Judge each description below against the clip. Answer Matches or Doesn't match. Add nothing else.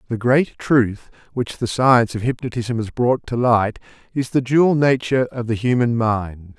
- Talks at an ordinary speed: Matches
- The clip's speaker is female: Doesn't match